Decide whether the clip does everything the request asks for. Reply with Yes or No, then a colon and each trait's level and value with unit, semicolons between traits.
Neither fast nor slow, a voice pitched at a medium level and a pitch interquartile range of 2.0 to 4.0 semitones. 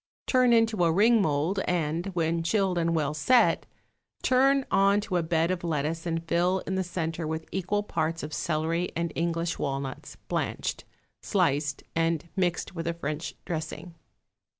Yes: average, 160 wpm; medium, 170 Hz; average, 2.8 semitones